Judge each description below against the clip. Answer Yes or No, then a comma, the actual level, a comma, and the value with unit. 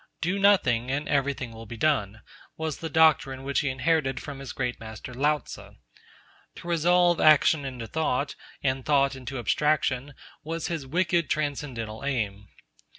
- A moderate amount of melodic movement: Yes, average, 3.8 semitones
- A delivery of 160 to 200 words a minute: No, average, 150 wpm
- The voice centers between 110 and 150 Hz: Yes, medium, 140 Hz